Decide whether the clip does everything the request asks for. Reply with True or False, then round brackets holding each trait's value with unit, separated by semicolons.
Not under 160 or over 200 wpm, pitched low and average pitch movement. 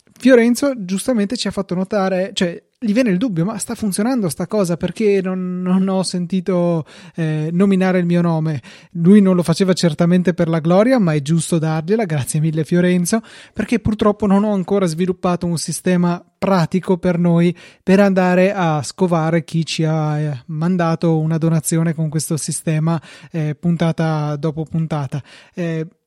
False (165 wpm; 175 Hz; 3.0 semitones)